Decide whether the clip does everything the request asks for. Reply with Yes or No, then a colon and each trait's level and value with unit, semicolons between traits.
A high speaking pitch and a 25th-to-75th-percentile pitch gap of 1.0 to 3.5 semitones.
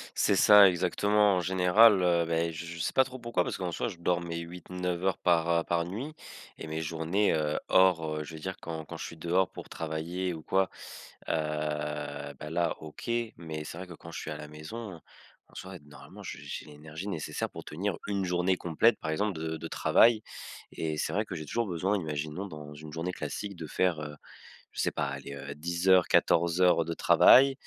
No: very low, 85 Hz; average, 2.9 semitones